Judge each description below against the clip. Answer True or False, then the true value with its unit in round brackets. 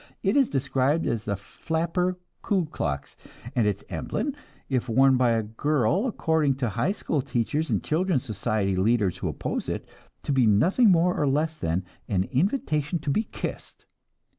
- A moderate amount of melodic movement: False (6.9 semitones)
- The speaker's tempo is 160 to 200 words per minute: True (165 wpm)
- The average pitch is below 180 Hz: True (140 Hz)